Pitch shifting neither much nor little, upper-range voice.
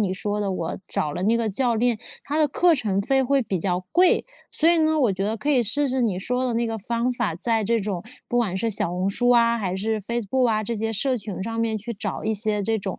Yes: average, 3.5 semitones; high, 225 Hz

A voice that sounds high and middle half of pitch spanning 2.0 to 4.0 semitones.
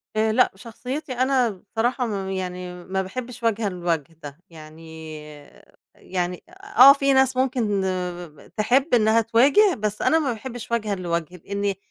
No: high, 215 Hz; wide, 5.6 semitones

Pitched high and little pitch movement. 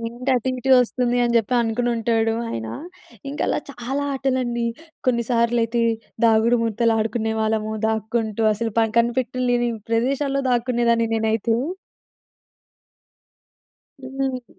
Yes: high, 235 Hz; narrow, 1.9 semitones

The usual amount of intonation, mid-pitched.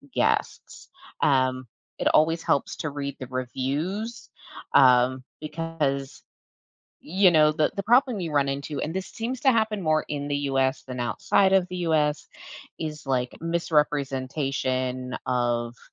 Yes: average, 4.4 semitones; medium, 145 Hz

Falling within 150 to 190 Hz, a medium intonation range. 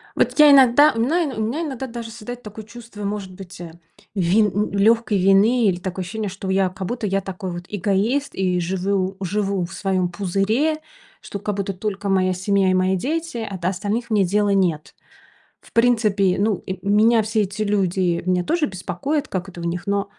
No: high, 200 Hz; average, 3.2 semitones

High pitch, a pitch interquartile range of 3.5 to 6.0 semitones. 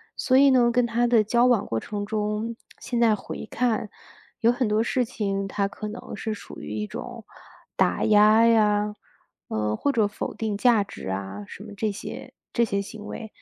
No: high, 215 Hz; narrow, 2.5 semitones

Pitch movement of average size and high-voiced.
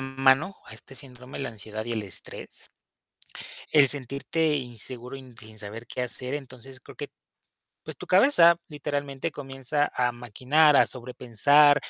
No: average, 3.1 semitones; low, 135 Hz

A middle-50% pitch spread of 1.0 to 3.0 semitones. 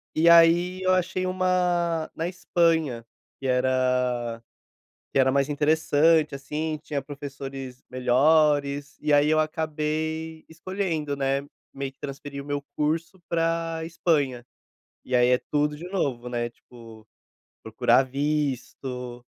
No: average, 3.6 semitones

